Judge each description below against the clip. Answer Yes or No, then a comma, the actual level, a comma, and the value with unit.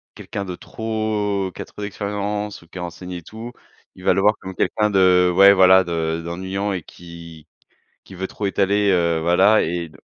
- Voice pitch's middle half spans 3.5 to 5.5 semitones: No, average, 2.8 semitones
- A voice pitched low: Yes, very low, 95 Hz